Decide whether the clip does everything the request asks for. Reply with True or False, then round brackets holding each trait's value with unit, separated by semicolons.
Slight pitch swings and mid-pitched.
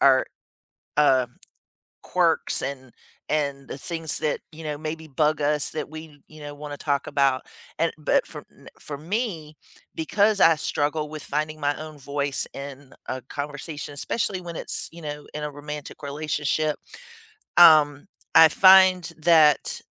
True (1.7 semitones; 150 Hz)